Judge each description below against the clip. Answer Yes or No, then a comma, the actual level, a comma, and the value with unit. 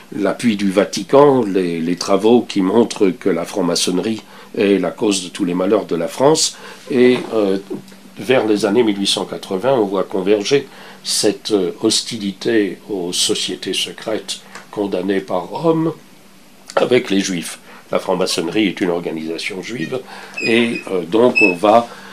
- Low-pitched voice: Yes, low, 105 Hz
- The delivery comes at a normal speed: No, slow, 140 wpm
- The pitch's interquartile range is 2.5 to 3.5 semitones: No, average, 4.1 semitones